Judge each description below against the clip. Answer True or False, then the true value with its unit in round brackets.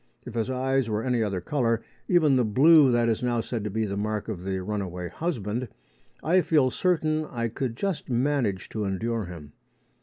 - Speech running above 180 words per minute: True (190 wpm)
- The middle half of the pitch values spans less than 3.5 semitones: False (4.3 semitones)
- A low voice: True (115 Hz)